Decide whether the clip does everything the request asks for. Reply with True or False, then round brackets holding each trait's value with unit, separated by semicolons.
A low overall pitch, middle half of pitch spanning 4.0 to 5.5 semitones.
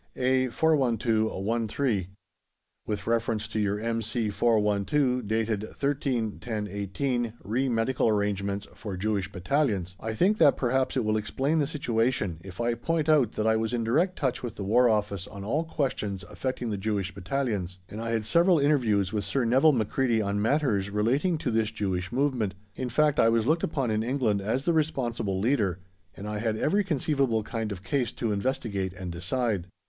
True (115 Hz; 4.3 semitones)